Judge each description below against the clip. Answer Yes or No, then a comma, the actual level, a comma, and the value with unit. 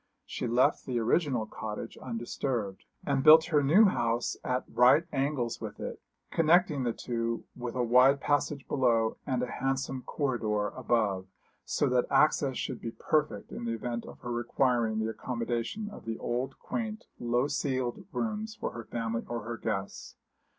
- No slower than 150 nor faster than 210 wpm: Yes, average, 165 wpm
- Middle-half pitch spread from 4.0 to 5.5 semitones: No, average, 3.4 semitones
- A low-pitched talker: Yes, low, 125 Hz